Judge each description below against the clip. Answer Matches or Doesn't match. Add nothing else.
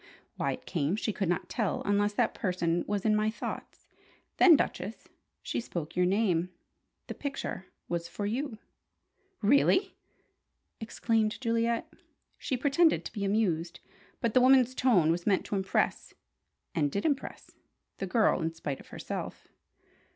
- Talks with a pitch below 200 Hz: Doesn't match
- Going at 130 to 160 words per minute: Matches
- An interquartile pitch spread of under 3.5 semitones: Doesn't match